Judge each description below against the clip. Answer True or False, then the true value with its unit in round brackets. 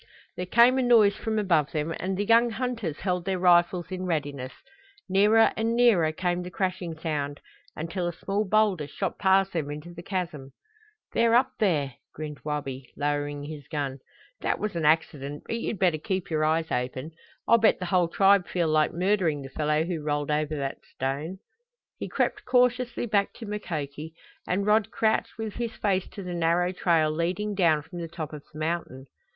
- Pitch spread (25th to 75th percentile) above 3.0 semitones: True (4.8 semitones)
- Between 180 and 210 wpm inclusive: True (185 wpm)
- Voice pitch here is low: False (175 Hz)